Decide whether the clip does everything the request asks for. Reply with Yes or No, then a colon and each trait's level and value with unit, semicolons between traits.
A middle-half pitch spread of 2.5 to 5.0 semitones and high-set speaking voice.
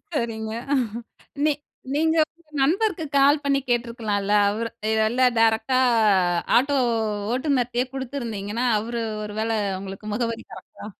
Yes: average, 3.9 semitones; high, 240 Hz